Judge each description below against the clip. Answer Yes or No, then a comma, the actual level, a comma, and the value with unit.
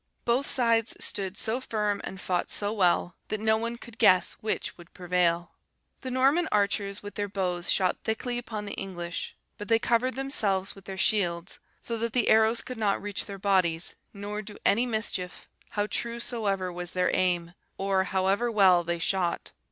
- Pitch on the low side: No, high, 205 Hz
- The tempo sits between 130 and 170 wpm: No, average, 180 wpm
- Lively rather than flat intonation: No, average, 3.5 semitones